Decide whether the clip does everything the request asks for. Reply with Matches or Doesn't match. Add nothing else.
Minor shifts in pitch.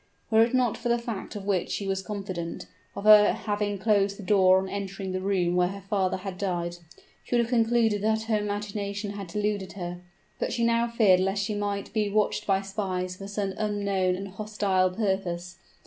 Matches